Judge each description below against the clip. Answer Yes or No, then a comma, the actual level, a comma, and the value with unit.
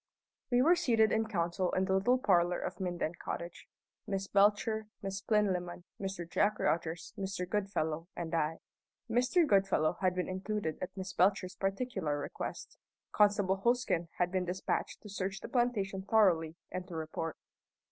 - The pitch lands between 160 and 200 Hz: Yes, high, 190 Hz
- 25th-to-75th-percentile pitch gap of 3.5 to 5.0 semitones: No, average, 3.1 semitones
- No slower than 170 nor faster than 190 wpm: No, average, 155 wpm